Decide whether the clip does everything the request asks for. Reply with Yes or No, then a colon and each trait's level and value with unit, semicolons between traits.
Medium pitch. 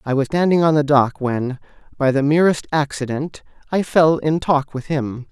Yes: medium, 145 Hz